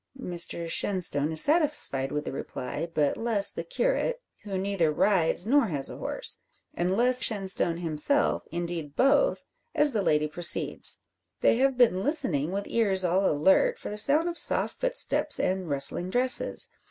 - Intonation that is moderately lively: No, wide, 7.5 semitones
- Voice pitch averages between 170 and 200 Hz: Yes, high, 190 Hz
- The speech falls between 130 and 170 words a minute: Yes, average, 160 wpm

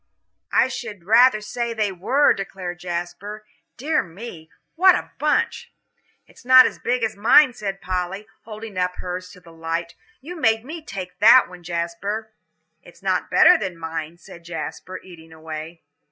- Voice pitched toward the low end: No, high, 195 Hz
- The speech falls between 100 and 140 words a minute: No, average, 160 wpm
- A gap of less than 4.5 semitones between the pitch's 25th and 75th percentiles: No, average, 5.0 semitones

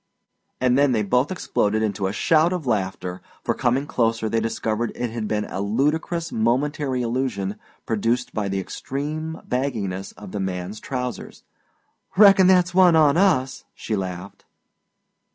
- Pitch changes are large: Yes, wide, 5.9 semitones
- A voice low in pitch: Yes, low, 120 Hz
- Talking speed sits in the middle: Yes, average, 150 wpm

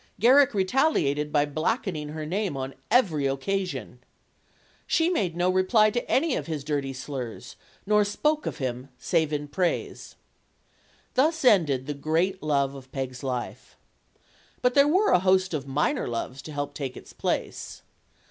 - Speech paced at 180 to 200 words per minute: No, average, 155 wpm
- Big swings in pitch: Yes, wide, 7.3 semitones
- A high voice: No, medium, 160 Hz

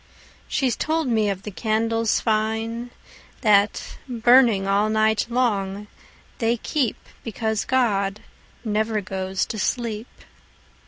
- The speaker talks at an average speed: No, slow, 100 wpm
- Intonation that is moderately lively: No, narrow, 2.2 semitones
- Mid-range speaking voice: No, high, 220 Hz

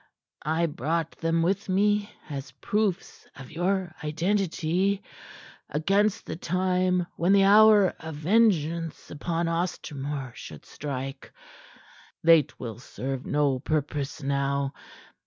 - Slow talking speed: Yes, slow, 110 wpm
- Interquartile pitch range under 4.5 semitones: No, average, 4.8 semitones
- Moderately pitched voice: Yes, medium, 165 Hz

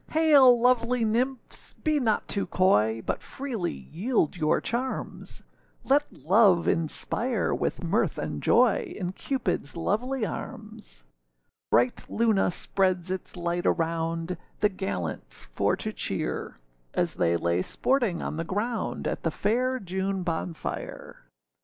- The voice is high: Yes, high, 195 Hz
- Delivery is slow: Yes, slow, 130 wpm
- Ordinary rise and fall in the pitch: No, wide, 6.6 semitones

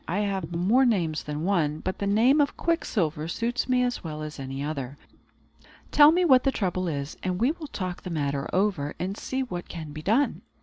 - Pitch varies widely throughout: Yes, wide, 8.0 semitones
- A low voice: No, medium, 185 Hz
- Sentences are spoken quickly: Yes, fast, 210 wpm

